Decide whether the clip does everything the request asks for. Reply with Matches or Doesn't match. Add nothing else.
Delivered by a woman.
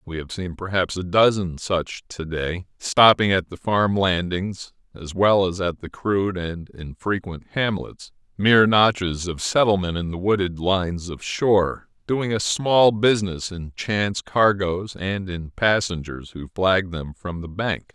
Doesn't match